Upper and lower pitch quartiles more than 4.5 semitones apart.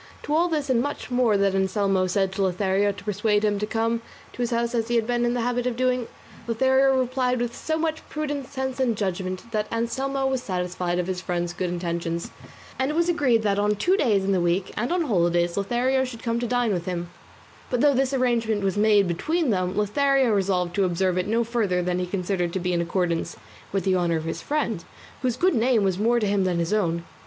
Yes: average, 5.2 semitones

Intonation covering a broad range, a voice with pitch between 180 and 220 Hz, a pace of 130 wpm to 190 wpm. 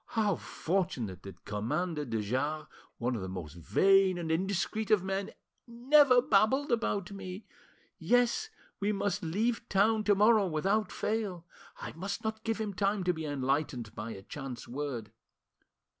Yes: wide, 7.4 semitones; high, 190 Hz; average, 155 wpm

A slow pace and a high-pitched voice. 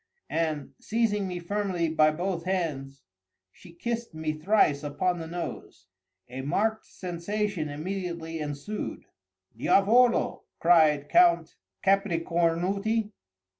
No: slow, 100 wpm; medium, 175 Hz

